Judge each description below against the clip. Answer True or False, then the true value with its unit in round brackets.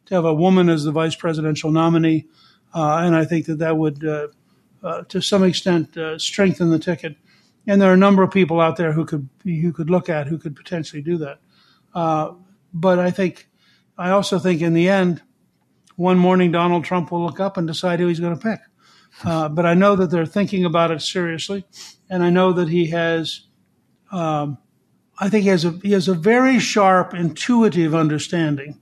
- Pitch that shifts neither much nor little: False (2.3 semitones)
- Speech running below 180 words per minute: False (205 wpm)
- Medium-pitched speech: True (170 Hz)